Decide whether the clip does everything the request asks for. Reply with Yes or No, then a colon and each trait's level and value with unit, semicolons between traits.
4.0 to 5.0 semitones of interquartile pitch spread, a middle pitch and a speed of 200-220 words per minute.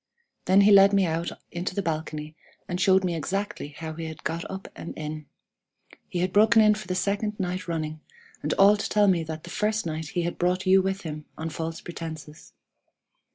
No: average, 3.5 semitones; medium, 175 Hz; fast, 205 wpm